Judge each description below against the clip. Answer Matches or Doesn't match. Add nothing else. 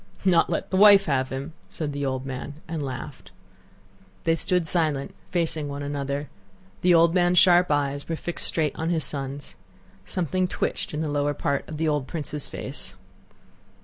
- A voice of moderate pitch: Matches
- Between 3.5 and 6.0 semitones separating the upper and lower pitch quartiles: Doesn't match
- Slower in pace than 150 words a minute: Doesn't match